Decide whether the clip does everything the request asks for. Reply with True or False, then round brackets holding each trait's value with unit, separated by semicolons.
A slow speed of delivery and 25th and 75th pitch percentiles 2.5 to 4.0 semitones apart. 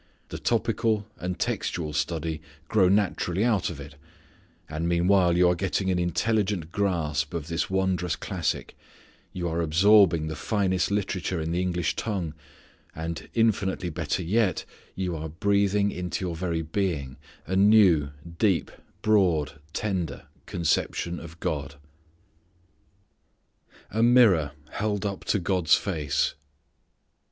True (125 wpm; 3.6 semitones)